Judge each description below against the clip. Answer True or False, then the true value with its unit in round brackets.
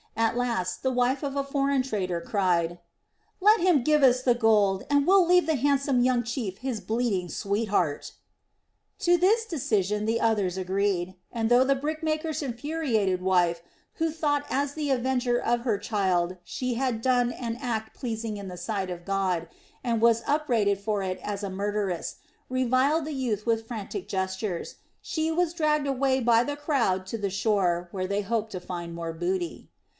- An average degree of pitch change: False (6.1 semitones)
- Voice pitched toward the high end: True (230 Hz)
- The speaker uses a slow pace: False (175 wpm)